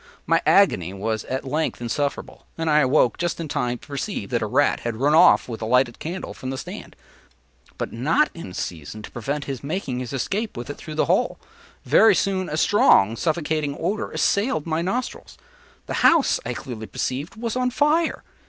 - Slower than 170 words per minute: No, average, 190 wpm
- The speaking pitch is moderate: Yes, medium, 145 Hz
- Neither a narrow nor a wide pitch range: No, wide, 6.8 semitones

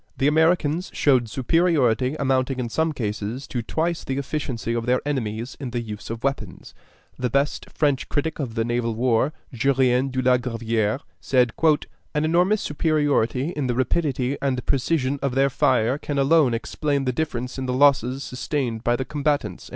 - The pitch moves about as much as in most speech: Yes, average, 3.2 semitones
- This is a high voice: No, low, 130 Hz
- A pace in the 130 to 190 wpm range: Yes, average, 170 wpm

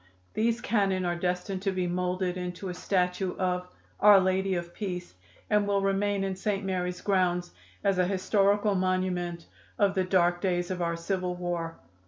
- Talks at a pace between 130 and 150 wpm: No, average, 170 wpm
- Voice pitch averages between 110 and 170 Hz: No, medium, 185 Hz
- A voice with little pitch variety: Yes, narrow, 1.6 semitones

